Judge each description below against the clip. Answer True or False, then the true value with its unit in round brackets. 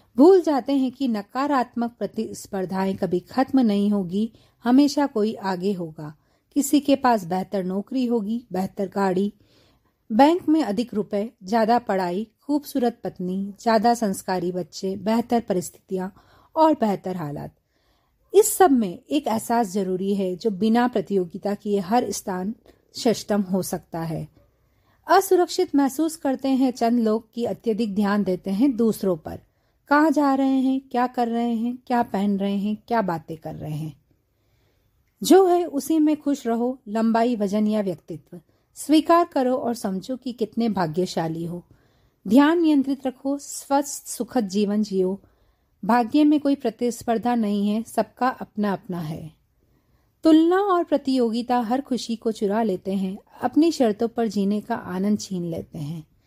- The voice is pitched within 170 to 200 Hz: False (225 Hz)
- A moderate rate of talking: True (145 wpm)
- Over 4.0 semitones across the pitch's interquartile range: True (5.2 semitones)